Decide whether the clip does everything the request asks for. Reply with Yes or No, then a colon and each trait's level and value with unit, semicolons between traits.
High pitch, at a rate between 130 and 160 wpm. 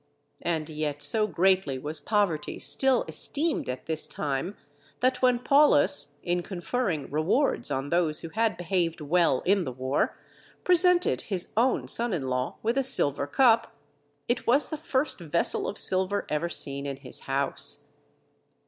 No: medium, 175 Hz; average, 155 wpm